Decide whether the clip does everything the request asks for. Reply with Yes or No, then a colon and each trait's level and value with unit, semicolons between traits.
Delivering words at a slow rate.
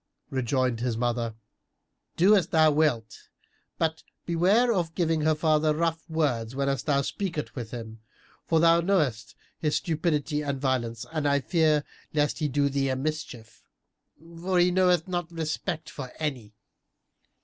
No: average, 150 wpm